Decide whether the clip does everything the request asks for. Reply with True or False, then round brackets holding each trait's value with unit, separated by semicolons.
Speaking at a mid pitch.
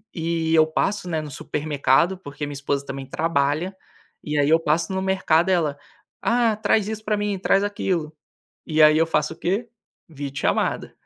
True (160 Hz)